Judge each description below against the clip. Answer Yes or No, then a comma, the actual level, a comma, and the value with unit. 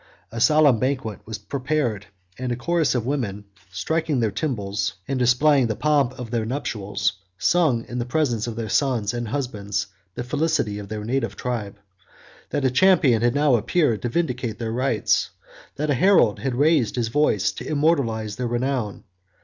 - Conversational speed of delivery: Yes, average, 175 wpm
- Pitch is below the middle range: Yes, low, 125 Hz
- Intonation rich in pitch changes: No, average, 4.5 semitones